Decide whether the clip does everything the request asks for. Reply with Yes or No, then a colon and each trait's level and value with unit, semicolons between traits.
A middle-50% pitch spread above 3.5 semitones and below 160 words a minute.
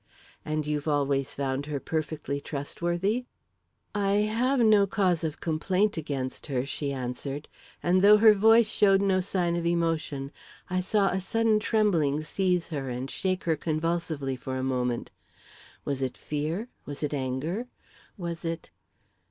Yes: wide, 5.6 semitones; average, 150 wpm